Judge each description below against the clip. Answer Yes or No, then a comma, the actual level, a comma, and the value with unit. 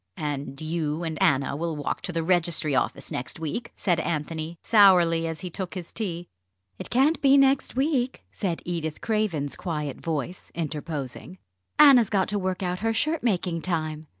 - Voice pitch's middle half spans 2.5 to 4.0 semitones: No, average, 4.5 semitones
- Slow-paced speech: No, average, 170 wpm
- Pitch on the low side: No, medium, 170 Hz